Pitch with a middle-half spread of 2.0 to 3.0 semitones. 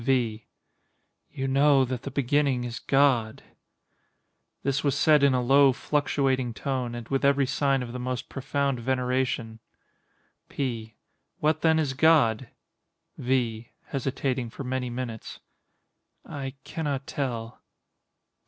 Yes: narrow, 2.4 semitones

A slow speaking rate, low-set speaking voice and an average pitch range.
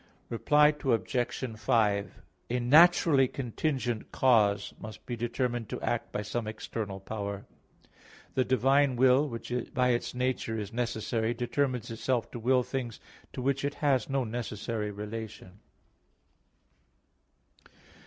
Yes: slow, 125 wpm; low, 120 Hz; average, 3.0 semitones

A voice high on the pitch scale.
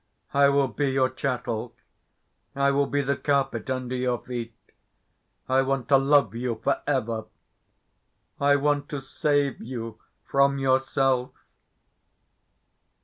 No: low, 135 Hz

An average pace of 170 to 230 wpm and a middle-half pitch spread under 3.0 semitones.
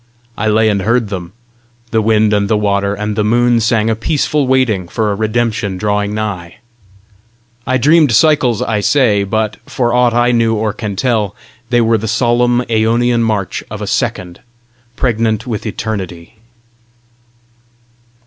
No: average, 155 wpm; narrow, 2.6 semitones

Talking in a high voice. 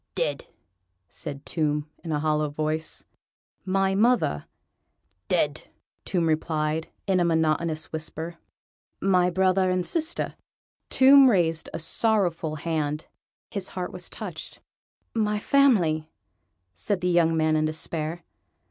No: medium, 165 Hz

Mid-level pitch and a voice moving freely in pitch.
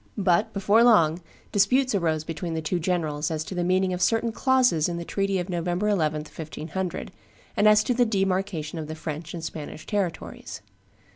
No: medium, 180 Hz; average, 4.2 semitones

